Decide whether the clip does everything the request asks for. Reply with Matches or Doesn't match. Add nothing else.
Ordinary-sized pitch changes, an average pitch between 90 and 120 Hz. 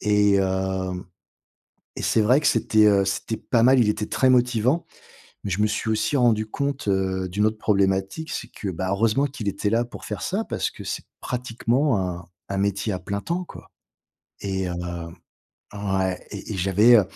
Matches